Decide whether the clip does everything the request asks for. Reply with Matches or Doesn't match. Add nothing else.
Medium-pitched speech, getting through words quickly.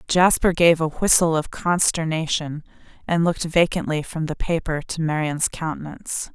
Doesn't match